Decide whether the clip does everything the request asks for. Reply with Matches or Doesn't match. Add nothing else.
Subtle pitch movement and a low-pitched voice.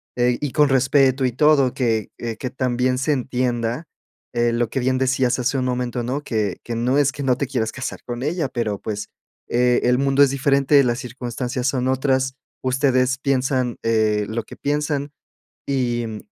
Matches